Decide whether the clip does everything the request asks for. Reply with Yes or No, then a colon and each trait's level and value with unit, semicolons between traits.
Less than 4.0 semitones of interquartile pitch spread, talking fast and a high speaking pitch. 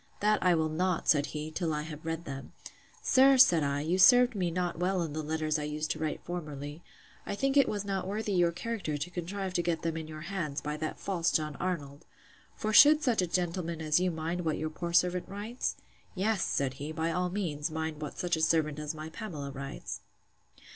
No: average, 3.3 semitones; fast, 215 wpm; medium, 165 Hz